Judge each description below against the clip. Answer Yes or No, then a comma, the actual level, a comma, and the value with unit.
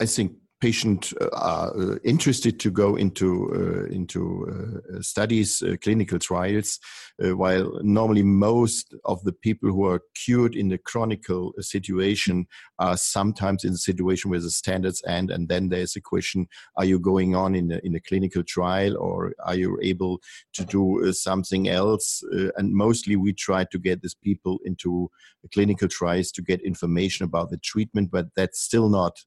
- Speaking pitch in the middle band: No, very low, 95 Hz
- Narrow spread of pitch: Yes, narrow, 2.1 semitones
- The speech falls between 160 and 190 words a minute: Yes, average, 180 wpm